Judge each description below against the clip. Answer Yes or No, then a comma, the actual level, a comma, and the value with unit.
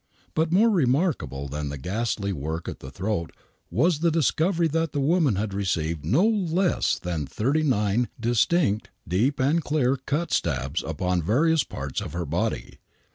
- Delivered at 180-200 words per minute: No, average, 160 wpm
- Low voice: Yes, low, 115 Hz